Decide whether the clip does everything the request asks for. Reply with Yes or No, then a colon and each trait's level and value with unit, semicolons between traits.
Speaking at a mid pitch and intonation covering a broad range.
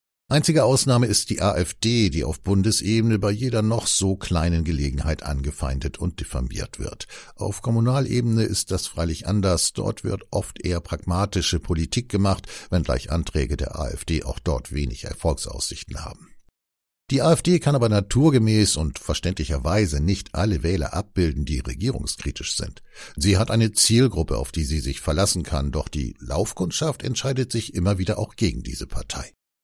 No: very low, 95 Hz; wide, 5.9 semitones